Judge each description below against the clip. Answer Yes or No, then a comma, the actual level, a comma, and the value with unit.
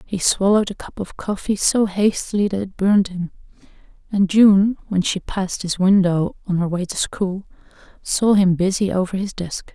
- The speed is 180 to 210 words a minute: Yes, average, 185 wpm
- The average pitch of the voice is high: Yes, high, 195 Hz